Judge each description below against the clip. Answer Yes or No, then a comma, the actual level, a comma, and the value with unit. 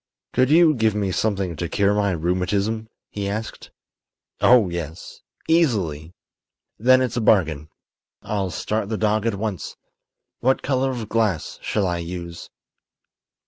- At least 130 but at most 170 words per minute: Yes, average, 140 wpm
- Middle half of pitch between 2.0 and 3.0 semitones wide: No, average, 4.2 semitones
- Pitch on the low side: Yes, low, 105 Hz